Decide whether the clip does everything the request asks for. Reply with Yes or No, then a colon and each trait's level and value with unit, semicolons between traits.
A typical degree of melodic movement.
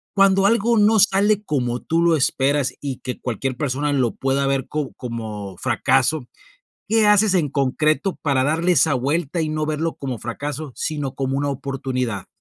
Yes: average, 4.2 semitones